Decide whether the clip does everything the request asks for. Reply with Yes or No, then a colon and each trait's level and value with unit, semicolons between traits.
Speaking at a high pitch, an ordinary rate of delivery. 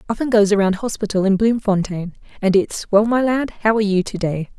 Yes: high, 205 Hz; average, 195 wpm